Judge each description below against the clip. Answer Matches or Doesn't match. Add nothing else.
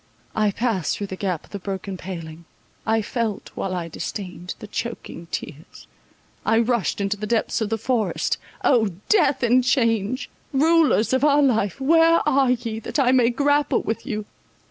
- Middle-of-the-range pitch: Doesn't match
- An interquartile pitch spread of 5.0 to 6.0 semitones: Doesn't match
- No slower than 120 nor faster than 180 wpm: Matches